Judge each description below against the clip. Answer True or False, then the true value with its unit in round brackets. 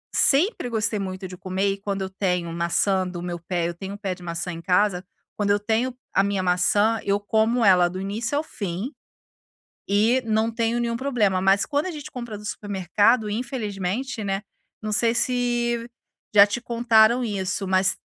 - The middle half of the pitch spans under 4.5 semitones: True (3.7 semitones)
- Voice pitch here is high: True (205 Hz)